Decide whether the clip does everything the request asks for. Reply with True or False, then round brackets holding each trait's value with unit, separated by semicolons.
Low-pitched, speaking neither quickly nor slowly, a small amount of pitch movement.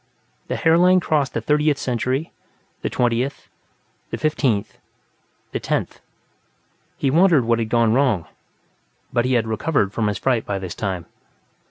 False (125 Hz; 145 wpm; 5.1 semitones)